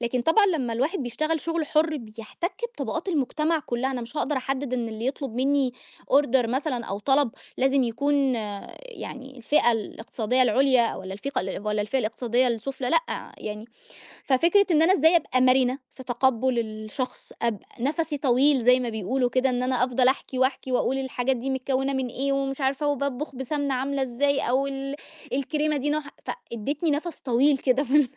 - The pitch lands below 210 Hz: No, very high, 265 Hz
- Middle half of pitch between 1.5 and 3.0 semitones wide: Yes, average, 2.7 semitones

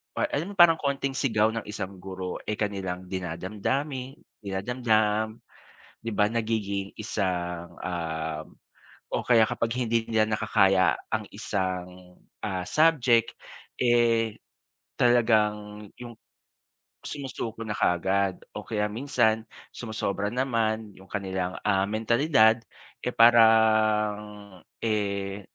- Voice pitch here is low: Yes, low, 105 Hz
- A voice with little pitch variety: No, average, 3.1 semitones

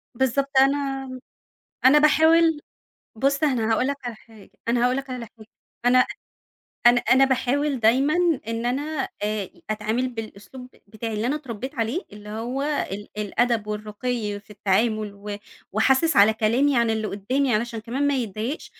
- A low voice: No, high, 240 Hz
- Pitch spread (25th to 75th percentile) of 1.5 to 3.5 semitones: No, average, 4.0 semitones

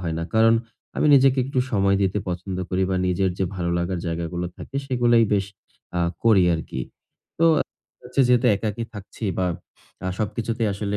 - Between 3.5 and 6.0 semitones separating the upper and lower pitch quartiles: Yes, average, 4.2 semitones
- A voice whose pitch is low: Yes, low, 100 Hz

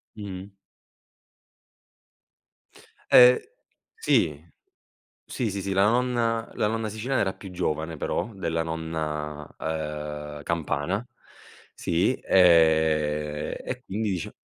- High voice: No, very low, 85 Hz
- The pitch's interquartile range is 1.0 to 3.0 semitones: No, wide, 5.5 semitones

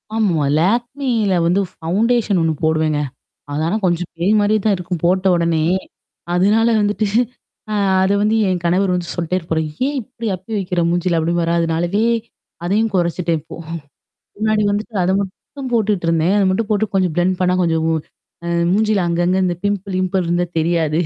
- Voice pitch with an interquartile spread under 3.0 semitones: No, average, 3.4 semitones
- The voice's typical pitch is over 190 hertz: No, medium, 185 Hz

